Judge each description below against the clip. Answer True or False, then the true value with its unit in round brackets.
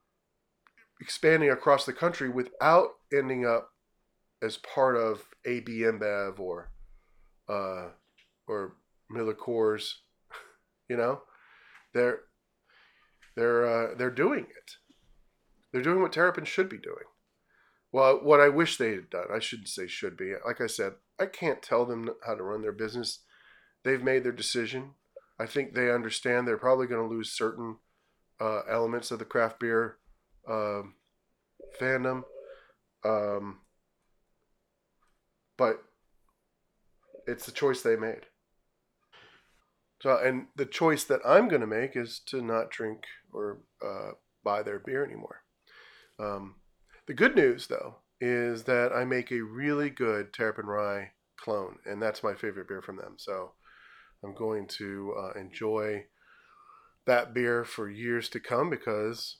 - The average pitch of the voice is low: True (120 Hz)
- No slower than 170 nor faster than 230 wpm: False (140 wpm)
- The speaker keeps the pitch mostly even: False (3.6 semitones)